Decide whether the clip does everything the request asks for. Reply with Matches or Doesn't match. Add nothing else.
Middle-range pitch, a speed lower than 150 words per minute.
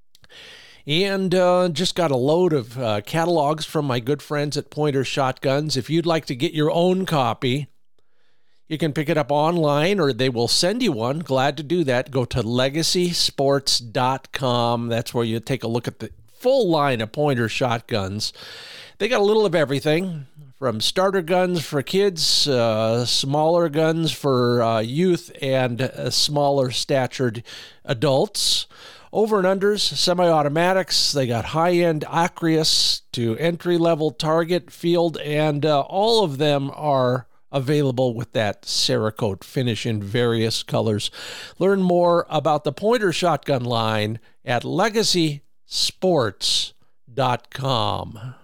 Matches